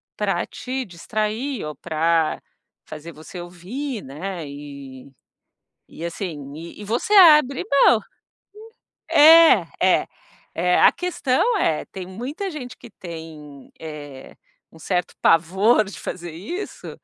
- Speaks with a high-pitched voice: No, medium, 180 Hz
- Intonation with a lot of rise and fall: Yes, wide, 8.2 semitones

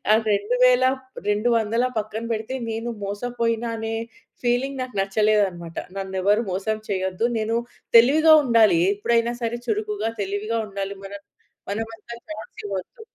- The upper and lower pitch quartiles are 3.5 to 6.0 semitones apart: No, average, 2.9 semitones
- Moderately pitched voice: No, high, 225 Hz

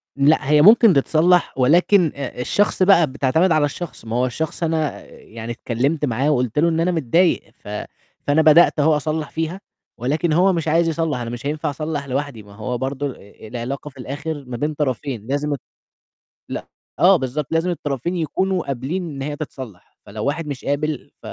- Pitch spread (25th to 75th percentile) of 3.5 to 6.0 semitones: Yes, average, 3.8 semitones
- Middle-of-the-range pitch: Yes, medium, 150 Hz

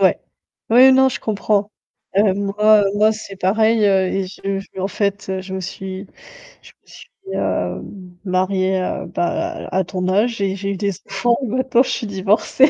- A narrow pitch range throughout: Yes, narrow, 2.3 semitones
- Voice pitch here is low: No, high, 200 Hz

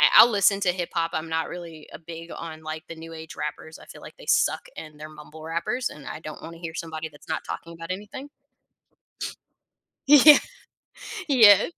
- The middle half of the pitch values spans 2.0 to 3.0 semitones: Yes, average, 2.7 semitones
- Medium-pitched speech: Yes, medium, 165 Hz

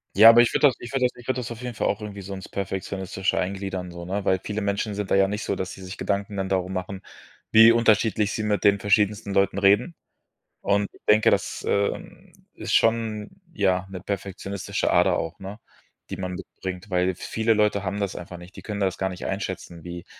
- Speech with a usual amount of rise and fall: No, narrow, 2.1 semitones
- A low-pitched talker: Yes, low, 100 Hz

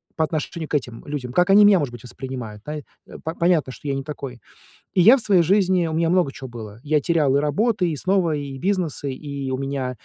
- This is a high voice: No, medium, 150 Hz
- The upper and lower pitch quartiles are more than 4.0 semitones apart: Yes, average, 5.0 semitones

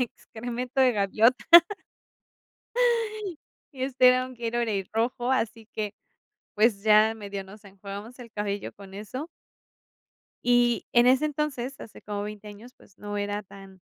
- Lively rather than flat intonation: No, average, 3.4 semitones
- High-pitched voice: Yes, high, 220 Hz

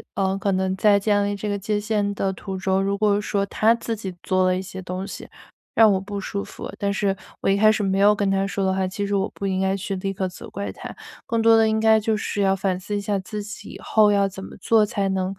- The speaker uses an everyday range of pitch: No, narrow, 1.4 semitones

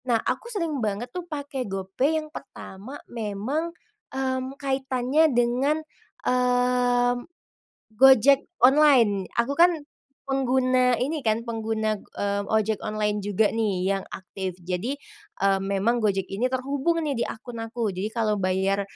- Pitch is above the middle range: Yes, high, 240 Hz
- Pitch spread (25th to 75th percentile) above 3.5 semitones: Yes, average, 4.4 semitones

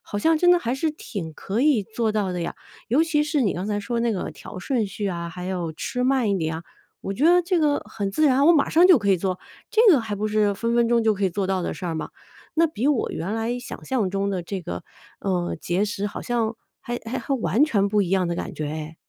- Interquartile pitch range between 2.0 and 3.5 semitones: No, wide, 5.4 semitones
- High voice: Yes, high, 210 Hz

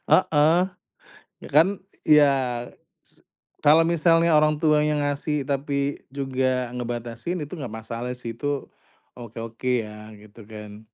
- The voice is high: No, medium, 140 Hz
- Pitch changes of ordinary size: Yes, average, 4.5 semitones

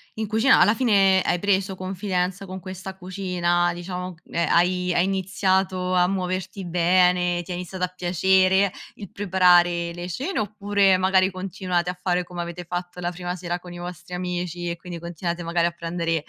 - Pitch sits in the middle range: Yes, medium, 180 Hz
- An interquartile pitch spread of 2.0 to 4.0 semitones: No, narrow, 1.4 semitones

